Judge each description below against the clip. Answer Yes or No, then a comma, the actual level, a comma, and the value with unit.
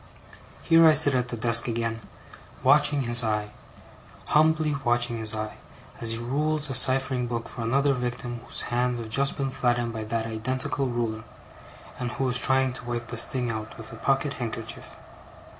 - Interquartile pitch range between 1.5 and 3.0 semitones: Yes, narrow, 2.6 semitones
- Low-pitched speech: Yes, low, 120 Hz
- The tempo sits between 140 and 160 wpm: No, average, 175 wpm